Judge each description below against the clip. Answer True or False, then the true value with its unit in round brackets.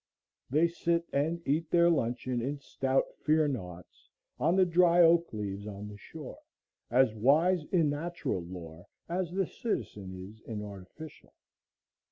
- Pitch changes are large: True (8.3 semitones)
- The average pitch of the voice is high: False (140 Hz)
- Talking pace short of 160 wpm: True (145 wpm)